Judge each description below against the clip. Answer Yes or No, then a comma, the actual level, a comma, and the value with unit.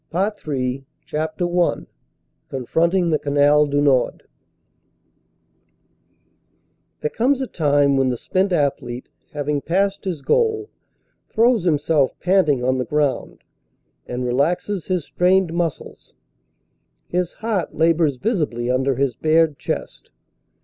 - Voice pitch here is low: No, medium, 155 Hz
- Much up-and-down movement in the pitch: No, average, 4.7 semitones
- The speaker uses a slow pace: Yes, slow, 115 wpm